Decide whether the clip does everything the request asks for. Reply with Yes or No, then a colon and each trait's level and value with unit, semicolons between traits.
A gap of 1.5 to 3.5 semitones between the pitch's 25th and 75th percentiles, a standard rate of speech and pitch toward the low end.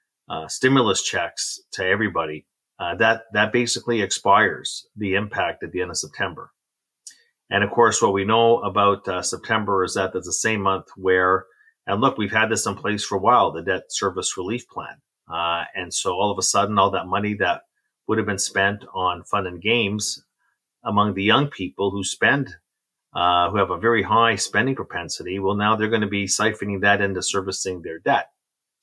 Yes: average, 2.8 semitones; average, 195 wpm; low, 100 Hz